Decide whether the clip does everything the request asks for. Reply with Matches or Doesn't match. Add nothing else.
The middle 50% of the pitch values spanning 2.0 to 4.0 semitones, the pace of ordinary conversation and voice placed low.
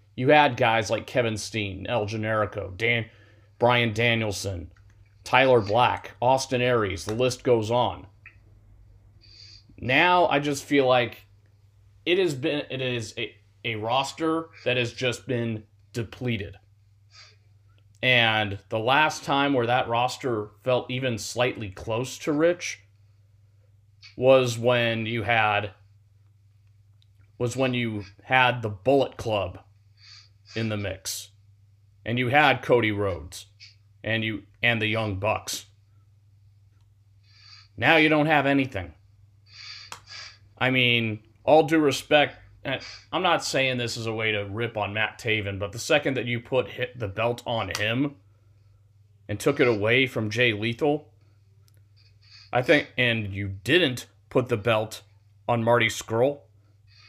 Doesn't match